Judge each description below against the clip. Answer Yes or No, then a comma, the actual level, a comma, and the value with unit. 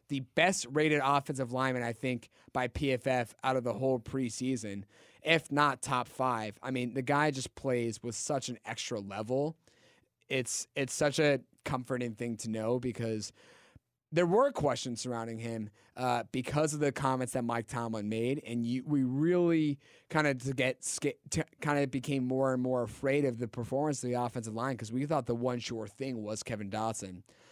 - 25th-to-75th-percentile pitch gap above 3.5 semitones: No, average, 3.0 semitones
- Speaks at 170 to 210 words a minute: Yes, average, 185 wpm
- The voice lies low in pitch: Yes, low, 130 Hz